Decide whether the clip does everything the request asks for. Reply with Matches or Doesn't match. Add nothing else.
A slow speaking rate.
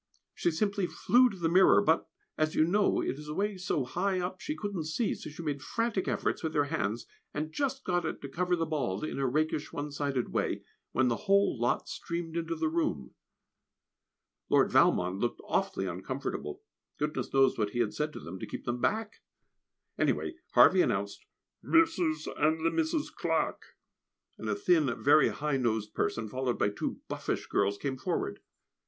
Doesn't match